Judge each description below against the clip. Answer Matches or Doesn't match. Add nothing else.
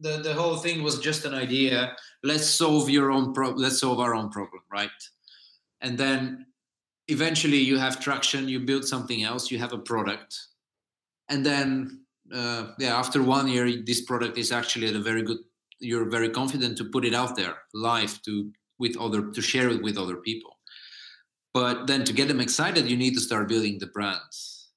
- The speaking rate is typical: Matches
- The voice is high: Doesn't match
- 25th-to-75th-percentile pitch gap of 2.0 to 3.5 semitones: Matches